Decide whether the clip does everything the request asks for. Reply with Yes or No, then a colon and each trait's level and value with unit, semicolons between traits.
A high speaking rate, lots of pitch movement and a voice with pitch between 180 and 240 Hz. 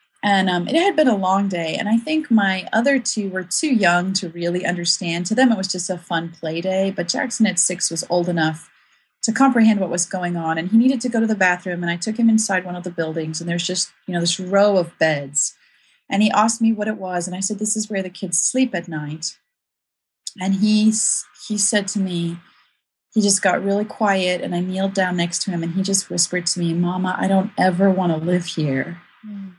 No: fast, 240 wpm; average, 3.5 semitones; medium, 185 Hz